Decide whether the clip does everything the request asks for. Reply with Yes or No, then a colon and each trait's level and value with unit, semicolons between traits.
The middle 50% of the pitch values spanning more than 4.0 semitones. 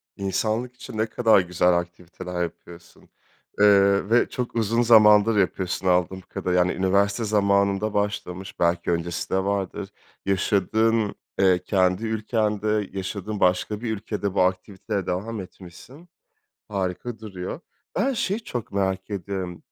No: average, 2.8 semitones